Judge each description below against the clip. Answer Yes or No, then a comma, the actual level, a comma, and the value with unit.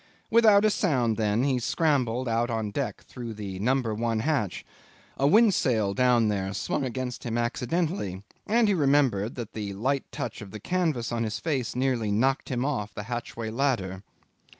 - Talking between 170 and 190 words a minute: Yes, average, 175 wpm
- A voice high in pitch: No, low, 120 Hz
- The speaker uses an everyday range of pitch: Yes, average, 4.3 semitones